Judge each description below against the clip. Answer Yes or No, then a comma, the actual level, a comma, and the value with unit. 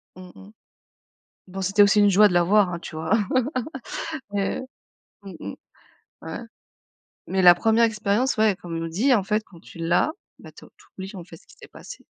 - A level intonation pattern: No, average, 3.2 semitones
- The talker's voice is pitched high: Yes, high, 195 Hz